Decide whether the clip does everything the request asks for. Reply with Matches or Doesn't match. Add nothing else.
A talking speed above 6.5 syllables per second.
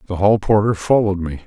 Matches